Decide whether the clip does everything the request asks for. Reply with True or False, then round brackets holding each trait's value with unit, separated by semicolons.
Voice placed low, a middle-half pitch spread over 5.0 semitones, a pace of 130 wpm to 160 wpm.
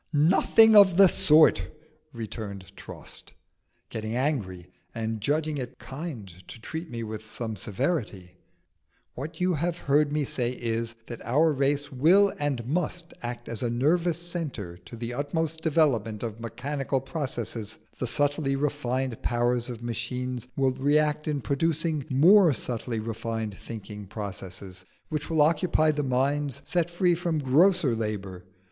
True (130 Hz; 5.4 semitones; 140 wpm)